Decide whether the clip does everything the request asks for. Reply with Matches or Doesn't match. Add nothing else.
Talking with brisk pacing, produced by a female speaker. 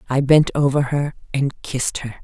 Doesn't match